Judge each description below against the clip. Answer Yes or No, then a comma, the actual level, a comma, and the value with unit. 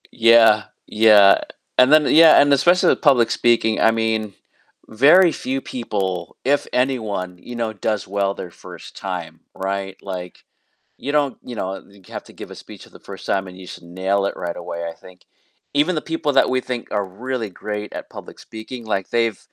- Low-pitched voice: Yes, low, 110 Hz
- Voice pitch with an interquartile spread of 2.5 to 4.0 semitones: No, average, 4.9 semitones